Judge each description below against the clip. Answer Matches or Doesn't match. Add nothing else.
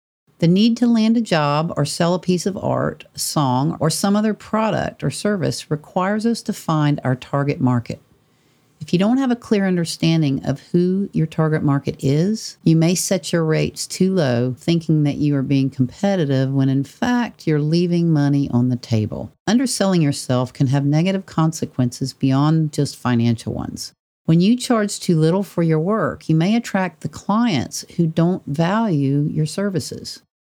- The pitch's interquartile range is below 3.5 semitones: Doesn't match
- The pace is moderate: Matches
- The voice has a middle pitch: Matches